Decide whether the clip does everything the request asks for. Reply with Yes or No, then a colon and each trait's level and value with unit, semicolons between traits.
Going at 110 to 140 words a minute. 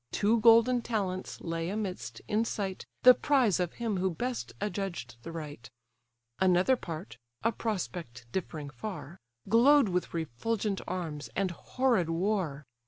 Yes: slow, 135 wpm